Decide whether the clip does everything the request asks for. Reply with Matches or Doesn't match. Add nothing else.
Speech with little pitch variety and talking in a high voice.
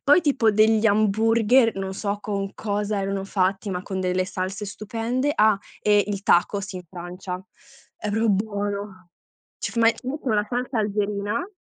Matches